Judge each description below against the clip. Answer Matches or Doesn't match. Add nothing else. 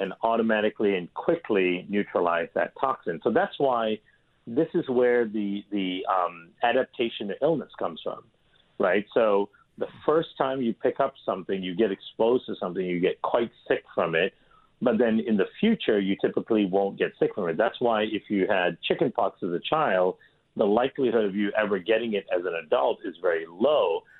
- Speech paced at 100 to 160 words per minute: Doesn't match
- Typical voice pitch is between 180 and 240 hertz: Doesn't match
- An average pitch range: Matches